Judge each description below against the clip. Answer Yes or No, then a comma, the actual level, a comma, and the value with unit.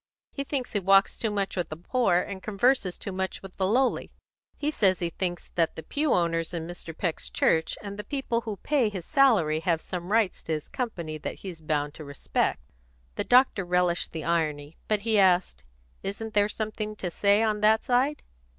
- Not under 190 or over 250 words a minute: Yes, average, 200 wpm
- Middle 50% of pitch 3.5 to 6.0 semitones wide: Yes, average, 4.6 semitones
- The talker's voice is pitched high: Yes, high, 195 Hz